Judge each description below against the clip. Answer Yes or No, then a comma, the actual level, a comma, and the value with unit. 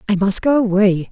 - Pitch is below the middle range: No, high, 200 Hz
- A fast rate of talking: Yes, fast, 215 wpm